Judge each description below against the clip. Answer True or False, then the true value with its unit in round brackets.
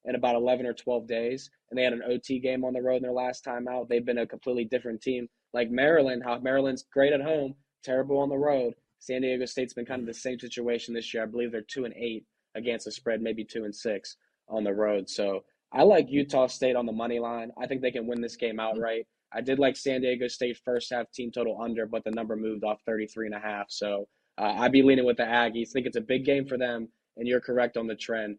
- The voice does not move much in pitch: True (2.0 semitones)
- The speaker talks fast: True (260 wpm)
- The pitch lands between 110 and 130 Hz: True (120 Hz)